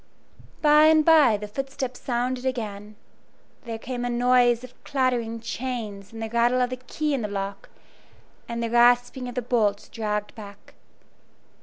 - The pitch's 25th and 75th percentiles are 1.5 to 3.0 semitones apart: Yes, narrow, 2.5 semitones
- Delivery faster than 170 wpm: No, average, 160 wpm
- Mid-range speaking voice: No, high, 240 Hz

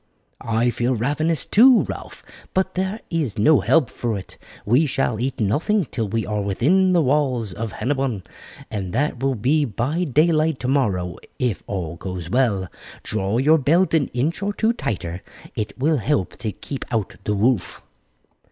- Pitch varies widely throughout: Yes, wide, 6.6 semitones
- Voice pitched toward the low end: Yes, low, 125 Hz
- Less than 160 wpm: No, average, 165 wpm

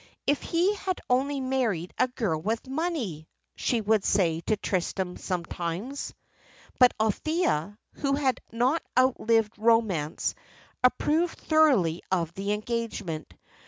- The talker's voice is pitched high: Yes, high, 225 Hz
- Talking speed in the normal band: No, slow, 120 wpm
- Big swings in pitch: Yes, wide, 6.6 semitones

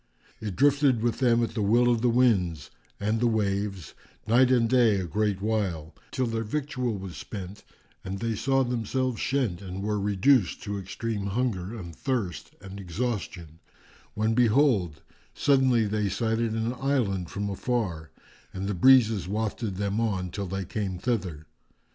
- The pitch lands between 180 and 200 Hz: No, low, 110 Hz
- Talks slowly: No, average, 160 wpm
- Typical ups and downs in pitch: Yes, average, 3.8 semitones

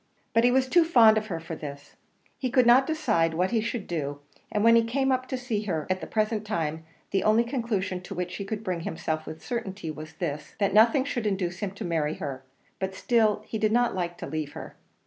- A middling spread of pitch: No, wide, 5.7 semitones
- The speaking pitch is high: Yes, high, 205 Hz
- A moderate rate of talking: No, fast, 235 wpm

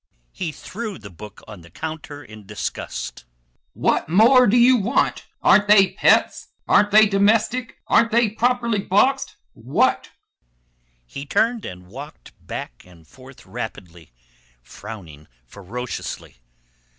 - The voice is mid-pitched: Yes, medium, 150 Hz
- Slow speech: Yes, slow, 125 wpm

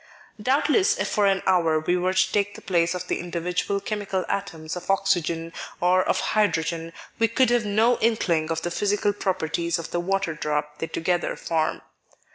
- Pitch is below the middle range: No, medium, 180 Hz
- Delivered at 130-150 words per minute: No, average, 180 wpm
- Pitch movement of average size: Yes, average, 3.5 semitones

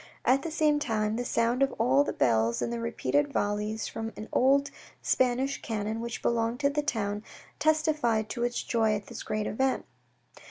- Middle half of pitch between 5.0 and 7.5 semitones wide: No, average, 4.2 semitones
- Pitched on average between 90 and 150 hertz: No, high, 235 Hz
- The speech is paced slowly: No, average, 185 wpm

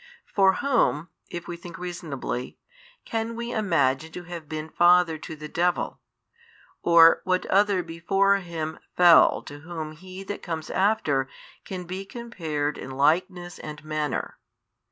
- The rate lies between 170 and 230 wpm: No, average, 140 wpm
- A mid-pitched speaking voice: Yes, medium, 175 Hz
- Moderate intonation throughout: Yes, average, 3.3 semitones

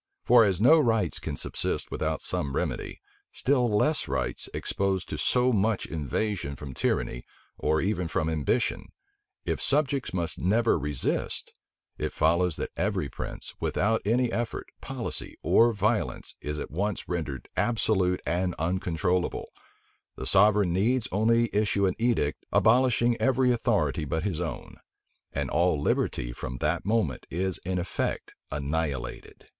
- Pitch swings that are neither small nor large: No, wide, 6.1 semitones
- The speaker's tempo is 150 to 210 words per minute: No, average, 140 wpm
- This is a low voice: Yes, very low, 95 Hz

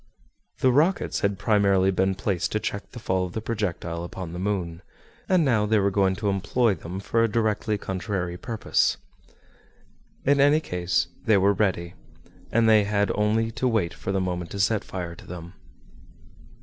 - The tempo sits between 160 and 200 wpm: Yes, average, 175 wpm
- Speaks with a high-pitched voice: No, low, 100 Hz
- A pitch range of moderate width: Yes, average, 3.3 semitones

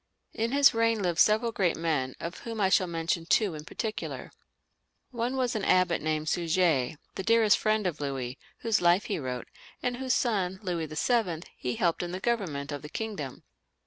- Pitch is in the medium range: Yes, medium, 180 Hz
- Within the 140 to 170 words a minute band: No, average, 190 wpm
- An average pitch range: No, wide, 5.9 semitones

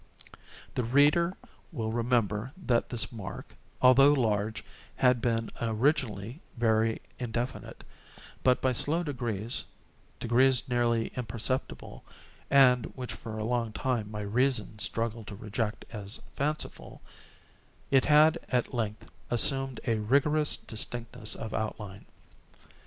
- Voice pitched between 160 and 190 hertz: No, low, 120 Hz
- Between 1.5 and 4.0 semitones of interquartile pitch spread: Yes, average, 3.1 semitones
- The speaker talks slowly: Yes, slow, 110 wpm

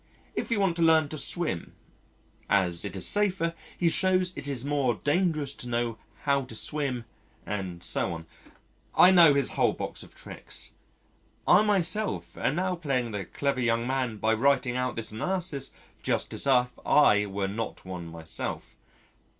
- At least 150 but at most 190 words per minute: Yes, average, 165 wpm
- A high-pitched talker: No, low, 135 Hz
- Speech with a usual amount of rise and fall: No, wide, 7.1 semitones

